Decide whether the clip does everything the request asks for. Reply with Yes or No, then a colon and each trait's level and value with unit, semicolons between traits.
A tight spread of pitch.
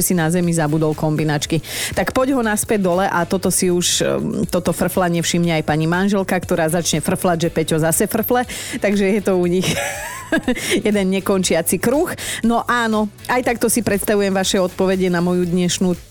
No: average, 3.7 semitones